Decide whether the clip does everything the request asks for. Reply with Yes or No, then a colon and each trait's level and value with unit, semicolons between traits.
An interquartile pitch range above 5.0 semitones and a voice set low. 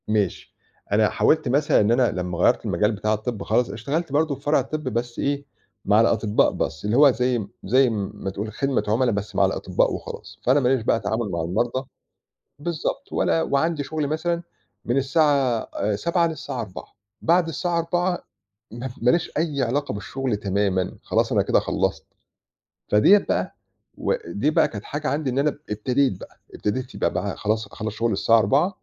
Yes: wide, 5.6 semitones; low, 125 Hz